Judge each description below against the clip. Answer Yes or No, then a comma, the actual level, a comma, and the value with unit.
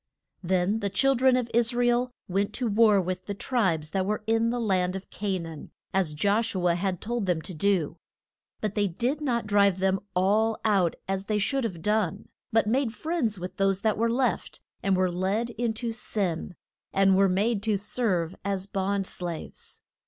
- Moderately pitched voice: No, high, 200 Hz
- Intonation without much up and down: No, average, 3.4 semitones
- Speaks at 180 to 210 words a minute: Yes, average, 195 wpm